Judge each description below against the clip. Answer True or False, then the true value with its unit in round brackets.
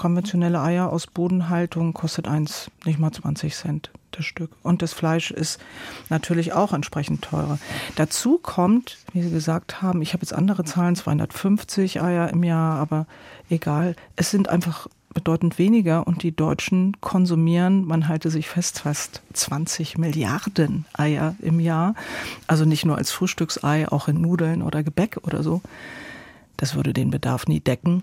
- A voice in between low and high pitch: True (165 Hz)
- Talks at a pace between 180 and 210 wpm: False (160 wpm)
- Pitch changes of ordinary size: False (2.2 semitones)